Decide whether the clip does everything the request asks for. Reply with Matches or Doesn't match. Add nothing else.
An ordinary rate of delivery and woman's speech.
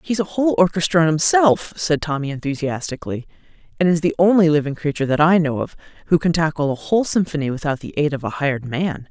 Doesn't match